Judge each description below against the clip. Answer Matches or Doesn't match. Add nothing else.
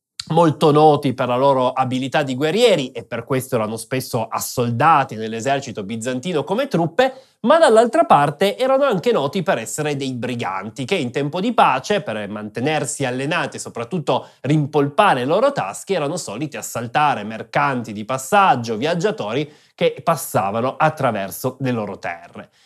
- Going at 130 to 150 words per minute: Matches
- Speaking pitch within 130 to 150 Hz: Matches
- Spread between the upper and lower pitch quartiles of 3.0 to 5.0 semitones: Doesn't match